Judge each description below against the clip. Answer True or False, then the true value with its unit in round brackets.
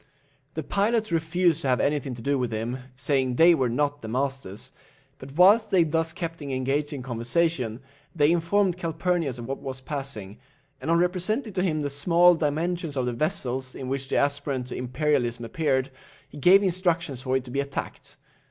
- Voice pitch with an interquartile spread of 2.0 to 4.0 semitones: False (4.5 semitones)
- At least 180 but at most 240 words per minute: True (190 wpm)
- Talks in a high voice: False (145 Hz)